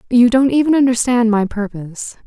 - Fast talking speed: No, average, 160 wpm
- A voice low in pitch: No, high, 235 Hz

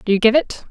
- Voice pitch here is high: Yes, high, 235 Hz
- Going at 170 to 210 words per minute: No, fast, 340 wpm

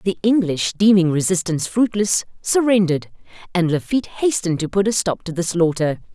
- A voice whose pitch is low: No, high, 190 Hz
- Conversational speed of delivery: Yes, average, 155 wpm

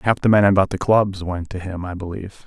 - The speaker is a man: Yes, male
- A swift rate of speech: Yes, fast, 270 wpm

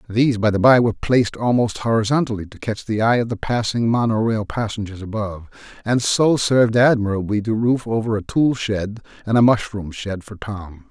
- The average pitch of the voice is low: Yes, low, 110 Hz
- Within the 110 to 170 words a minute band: No, average, 195 wpm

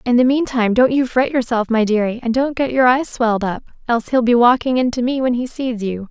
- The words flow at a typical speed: No, fast, 255 wpm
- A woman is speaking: Yes, female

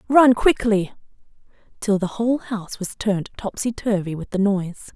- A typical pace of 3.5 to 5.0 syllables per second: No, 5.4 syllables/s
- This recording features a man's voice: No, female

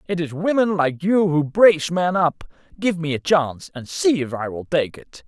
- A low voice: No, medium, 165 Hz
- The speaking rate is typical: No, fast, 230 wpm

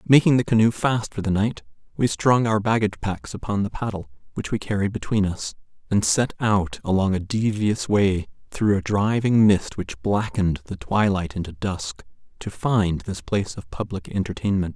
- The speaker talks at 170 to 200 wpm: Yes, average, 180 wpm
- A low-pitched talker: Yes, low, 105 Hz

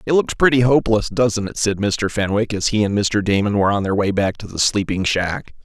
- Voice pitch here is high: No, low, 105 Hz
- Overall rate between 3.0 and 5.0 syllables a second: No, 5.5 syllables/s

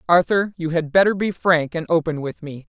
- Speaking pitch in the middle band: Yes, medium, 165 Hz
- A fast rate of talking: Yes, fast, 215 wpm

